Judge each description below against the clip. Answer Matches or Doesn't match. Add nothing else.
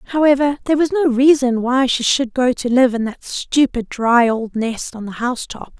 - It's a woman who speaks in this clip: Matches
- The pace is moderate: Doesn't match